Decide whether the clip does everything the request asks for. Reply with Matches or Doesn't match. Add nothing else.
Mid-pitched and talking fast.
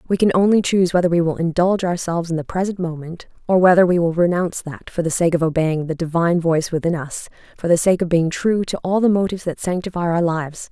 Matches